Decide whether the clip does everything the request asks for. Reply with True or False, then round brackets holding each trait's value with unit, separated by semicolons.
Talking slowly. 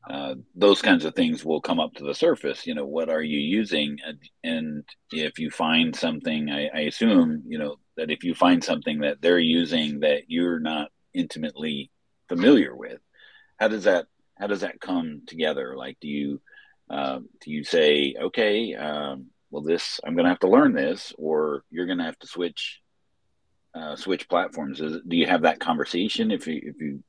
False (195 wpm)